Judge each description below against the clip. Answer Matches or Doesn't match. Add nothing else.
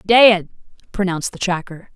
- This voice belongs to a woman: Matches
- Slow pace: Matches